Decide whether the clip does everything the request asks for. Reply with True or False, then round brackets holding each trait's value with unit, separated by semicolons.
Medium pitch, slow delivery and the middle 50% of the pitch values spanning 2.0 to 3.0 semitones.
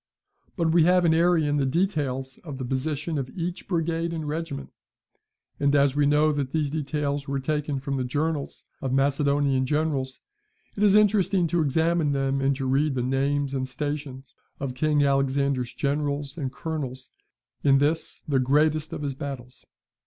False (145 Hz; 165 wpm; 2.6 semitones)